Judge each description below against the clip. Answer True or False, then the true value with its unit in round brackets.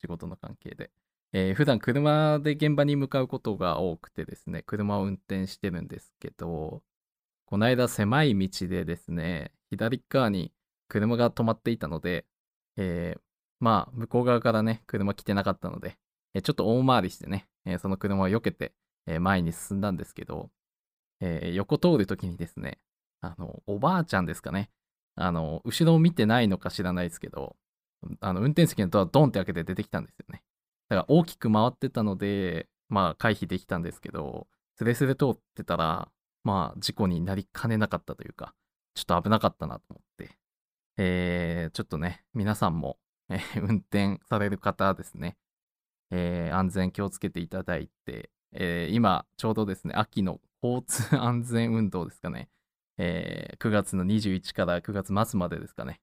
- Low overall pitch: True (100 Hz)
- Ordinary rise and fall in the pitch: True (4.1 semitones)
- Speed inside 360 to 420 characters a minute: False (335 characters per minute)